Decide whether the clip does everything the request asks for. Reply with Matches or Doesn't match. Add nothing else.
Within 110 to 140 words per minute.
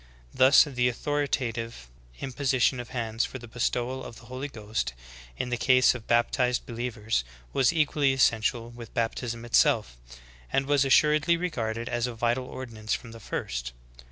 Doesn't match